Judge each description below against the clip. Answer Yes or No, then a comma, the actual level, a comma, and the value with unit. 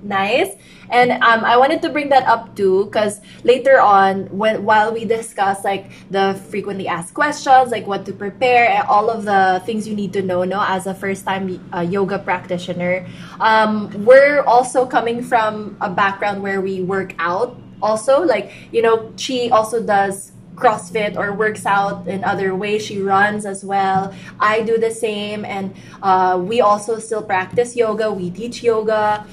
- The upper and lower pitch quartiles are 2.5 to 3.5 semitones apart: Yes, average, 2.8 semitones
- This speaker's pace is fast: No, average, 175 wpm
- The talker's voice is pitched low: No, high, 205 Hz